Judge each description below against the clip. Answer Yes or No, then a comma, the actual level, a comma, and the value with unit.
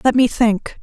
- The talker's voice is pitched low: No, high, 235 Hz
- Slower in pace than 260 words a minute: Yes, fast, 220 wpm